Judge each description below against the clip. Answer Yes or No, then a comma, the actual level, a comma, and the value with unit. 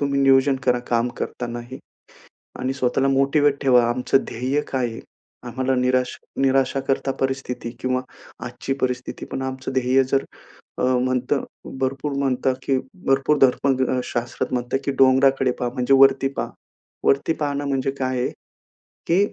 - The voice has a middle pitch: No, low, 130 Hz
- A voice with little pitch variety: Yes, narrow, 1.3 semitones